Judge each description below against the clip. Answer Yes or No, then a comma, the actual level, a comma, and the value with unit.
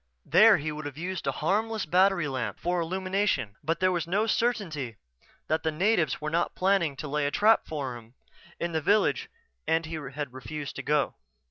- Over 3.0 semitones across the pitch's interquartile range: Yes, average, 4.4 semitones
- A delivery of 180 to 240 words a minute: Yes, average, 195 wpm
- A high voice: No, medium, 160 Hz